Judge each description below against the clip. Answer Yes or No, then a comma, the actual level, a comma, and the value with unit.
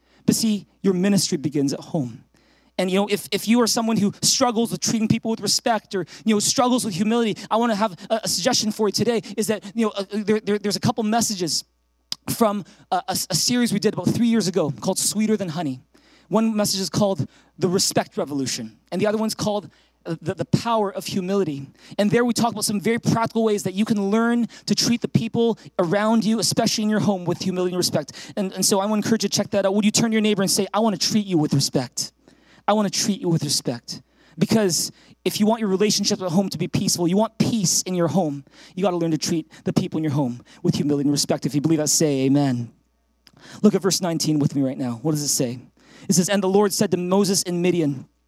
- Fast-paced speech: Yes, fast, 250 wpm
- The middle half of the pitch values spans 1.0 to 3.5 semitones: No, average, 4.2 semitones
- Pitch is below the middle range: No, high, 200 Hz